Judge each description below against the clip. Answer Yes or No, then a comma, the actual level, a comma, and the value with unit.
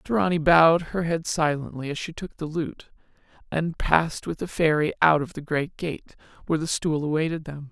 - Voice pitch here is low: No, medium, 160 Hz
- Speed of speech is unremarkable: Yes, average, 195 wpm